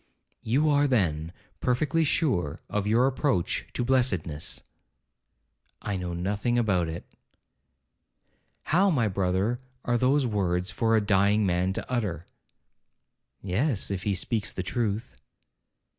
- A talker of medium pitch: No, low, 105 Hz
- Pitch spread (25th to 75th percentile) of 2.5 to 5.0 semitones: No, wide, 5.4 semitones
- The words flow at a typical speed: No, slow, 125 wpm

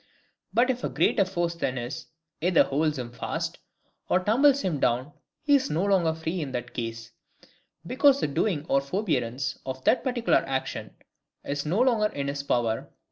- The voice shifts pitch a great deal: Yes, wide, 8.1 semitones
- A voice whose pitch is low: No, medium, 160 Hz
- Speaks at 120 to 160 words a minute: No, average, 175 wpm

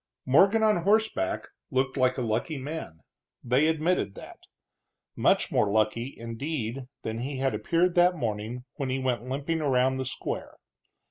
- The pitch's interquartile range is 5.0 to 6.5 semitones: Yes, average, 5.3 semitones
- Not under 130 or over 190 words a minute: Yes, average, 150 wpm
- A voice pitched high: No, low, 130 Hz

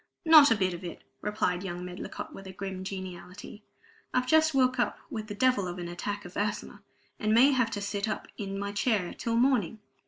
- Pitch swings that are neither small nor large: Yes, average, 4.2 semitones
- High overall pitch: Yes, high, 205 Hz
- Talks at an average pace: No, fast, 210 wpm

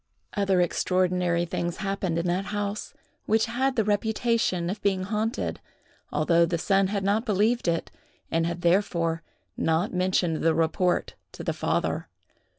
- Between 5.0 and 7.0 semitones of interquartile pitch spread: No, average, 3.3 semitones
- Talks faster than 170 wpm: No, average, 150 wpm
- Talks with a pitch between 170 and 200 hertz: Yes, medium, 185 Hz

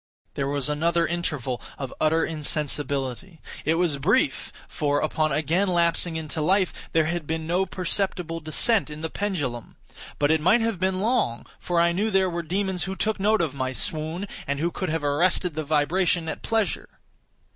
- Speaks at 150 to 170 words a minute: No, average, 180 wpm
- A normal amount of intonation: Yes, average, 3.8 semitones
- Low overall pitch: No, medium, 165 Hz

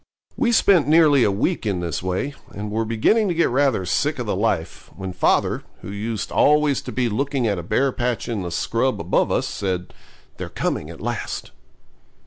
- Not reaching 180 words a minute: No, average, 195 wpm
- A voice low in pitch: Yes, low, 115 Hz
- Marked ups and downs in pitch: Yes, wide, 6.4 semitones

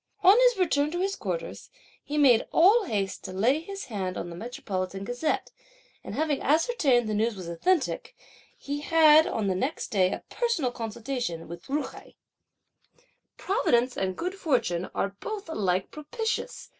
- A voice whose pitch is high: Yes, very high, 265 Hz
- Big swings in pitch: Yes, wide, 8.7 semitones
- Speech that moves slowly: No, average, 165 wpm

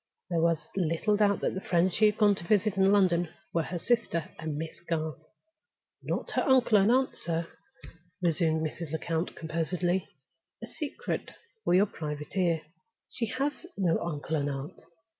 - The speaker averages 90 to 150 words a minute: No, average, 165 wpm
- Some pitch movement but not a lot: Yes, average, 4.0 semitones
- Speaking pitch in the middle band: Yes, medium, 175 Hz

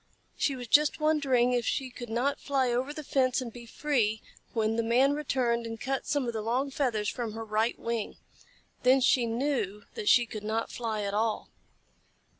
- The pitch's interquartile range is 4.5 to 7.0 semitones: No, average, 3.1 semitones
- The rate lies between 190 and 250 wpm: Yes, average, 195 wpm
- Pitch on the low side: No, high, 240 Hz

